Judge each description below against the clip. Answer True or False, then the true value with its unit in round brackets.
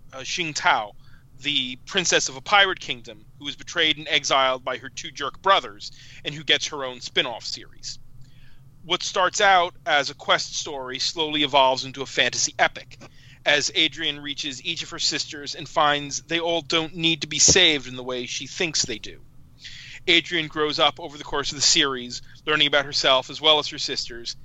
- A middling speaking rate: True (195 wpm)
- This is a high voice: False (145 Hz)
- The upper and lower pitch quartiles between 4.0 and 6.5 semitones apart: False (3.6 semitones)